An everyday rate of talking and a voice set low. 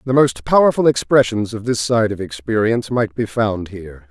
Yes: average, 190 wpm; low, 110 Hz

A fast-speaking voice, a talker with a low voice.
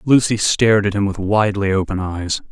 No: average, 190 wpm; low, 100 Hz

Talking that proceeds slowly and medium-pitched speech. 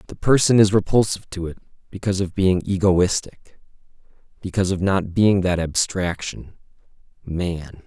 No: slow, 130 wpm; very low, 95 Hz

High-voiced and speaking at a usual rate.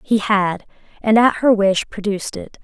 Yes: high, 210 Hz; average, 180 wpm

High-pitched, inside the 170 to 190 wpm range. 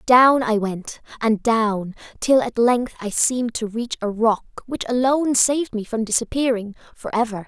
Yes: high, 230 Hz; average, 175 wpm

